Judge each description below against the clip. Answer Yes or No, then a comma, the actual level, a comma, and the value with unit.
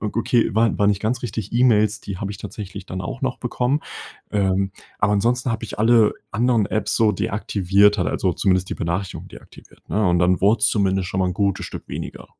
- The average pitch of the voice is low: Yes, low, 105 Hz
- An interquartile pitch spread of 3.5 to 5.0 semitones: No, average, 2.9 semitones